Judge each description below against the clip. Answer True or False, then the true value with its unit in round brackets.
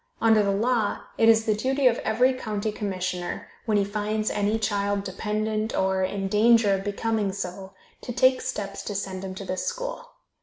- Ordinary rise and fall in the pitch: False (2.3 semitones)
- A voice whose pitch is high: True (210 Hz)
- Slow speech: False (185 wpm)